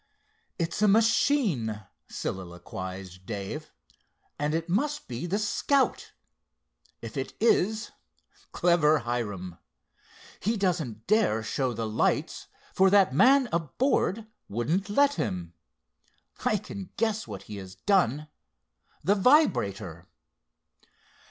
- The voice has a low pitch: No, medium, 165 Hz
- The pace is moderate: No, slow, 100 wpm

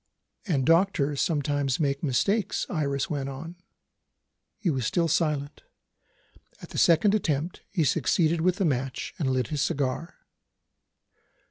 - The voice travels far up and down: No, average, 3.7 semitones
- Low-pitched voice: No, medium, 150 Hz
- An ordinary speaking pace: No, slow, 130 wpm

